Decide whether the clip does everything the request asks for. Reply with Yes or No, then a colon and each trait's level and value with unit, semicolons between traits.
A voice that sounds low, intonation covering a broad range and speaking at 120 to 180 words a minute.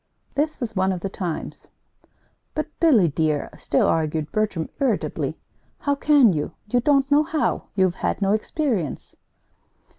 No: high, 215 Hz; wide, 8.8 semitones; average, 145 wpm